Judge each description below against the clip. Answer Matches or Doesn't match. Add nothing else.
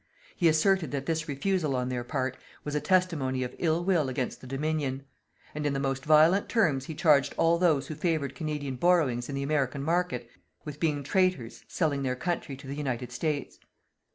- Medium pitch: Matches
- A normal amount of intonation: Matches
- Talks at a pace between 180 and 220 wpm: Matches